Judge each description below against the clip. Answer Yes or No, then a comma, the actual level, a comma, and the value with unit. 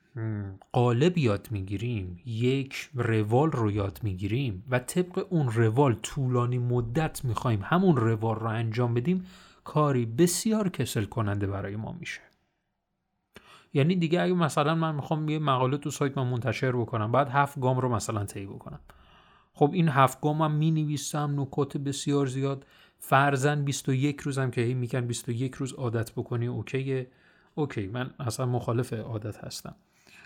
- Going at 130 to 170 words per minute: Yes, average, 145 wpm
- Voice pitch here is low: Yes, low, 130 Hz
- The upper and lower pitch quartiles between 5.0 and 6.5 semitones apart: No, average, 4.2 semitones